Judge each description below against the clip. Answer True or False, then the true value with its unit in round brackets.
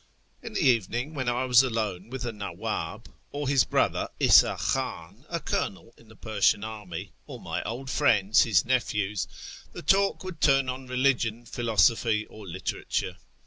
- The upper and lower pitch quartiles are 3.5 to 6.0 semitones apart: True (3.8 semitones)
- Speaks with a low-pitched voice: True (115 Hz)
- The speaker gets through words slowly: False (165 wpm)